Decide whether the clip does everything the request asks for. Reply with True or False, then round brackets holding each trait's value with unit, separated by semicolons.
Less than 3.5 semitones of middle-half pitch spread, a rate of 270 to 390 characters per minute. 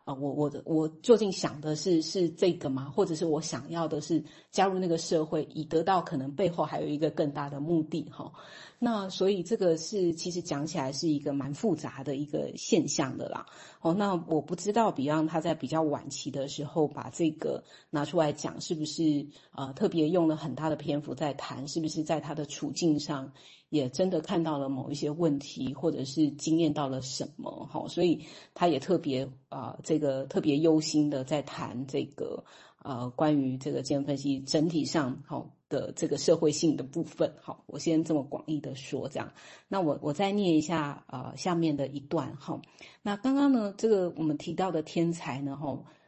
True (2.7 semitones; 290 characters per minute)